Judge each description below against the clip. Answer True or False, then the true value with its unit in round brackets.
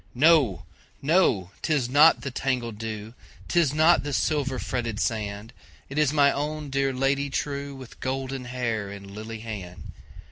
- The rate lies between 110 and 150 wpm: True (135 wpm)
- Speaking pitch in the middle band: False (130 Hz)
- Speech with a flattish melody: False (4.1 semitones)